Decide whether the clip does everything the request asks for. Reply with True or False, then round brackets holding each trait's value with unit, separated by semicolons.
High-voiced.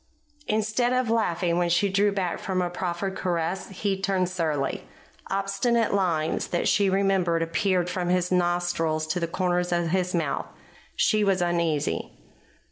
False (180 Hz)